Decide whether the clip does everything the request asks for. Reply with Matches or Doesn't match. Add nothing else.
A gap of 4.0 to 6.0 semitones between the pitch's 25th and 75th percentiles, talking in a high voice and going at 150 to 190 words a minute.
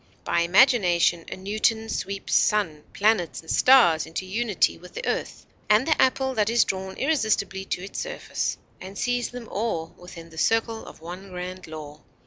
Matches